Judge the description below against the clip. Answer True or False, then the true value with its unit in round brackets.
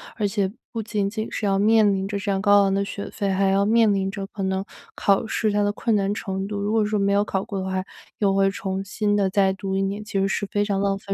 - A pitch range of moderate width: False (1.2 semitones)